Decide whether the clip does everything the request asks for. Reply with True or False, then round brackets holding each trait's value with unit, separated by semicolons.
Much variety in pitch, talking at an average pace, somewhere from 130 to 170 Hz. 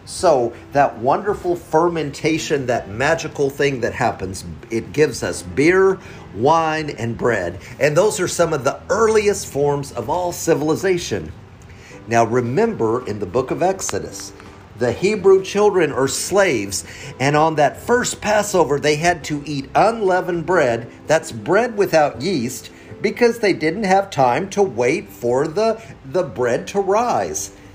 True (7.8 semitones; 145 wpm; 155 Hz)